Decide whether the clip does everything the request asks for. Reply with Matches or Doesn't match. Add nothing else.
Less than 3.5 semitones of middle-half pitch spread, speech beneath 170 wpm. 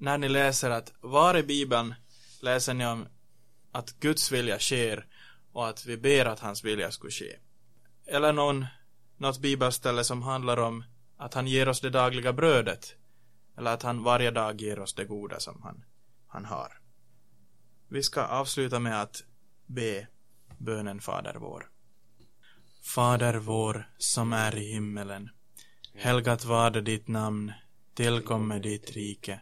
Matches